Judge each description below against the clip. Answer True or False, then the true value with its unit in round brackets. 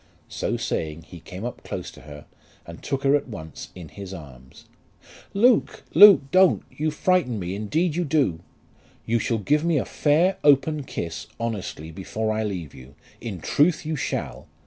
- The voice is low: True (115 Hz)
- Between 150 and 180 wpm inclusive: True (170 wpm)